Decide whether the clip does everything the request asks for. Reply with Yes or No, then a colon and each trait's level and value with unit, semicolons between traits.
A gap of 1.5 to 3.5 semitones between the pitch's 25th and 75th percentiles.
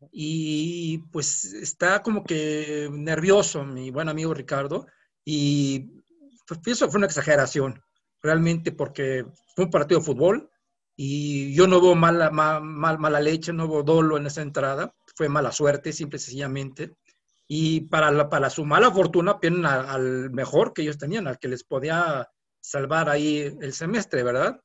Yes: average, 2.7 semitones